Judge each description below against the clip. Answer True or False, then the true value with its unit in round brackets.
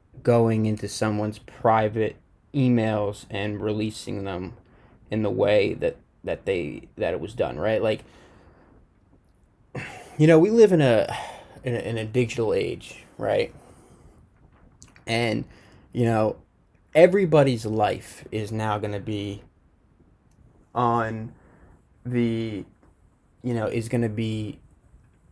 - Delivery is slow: True (120 wpm)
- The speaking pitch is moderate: False (110 Hz)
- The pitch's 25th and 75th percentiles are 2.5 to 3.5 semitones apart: True (2.9 semitones)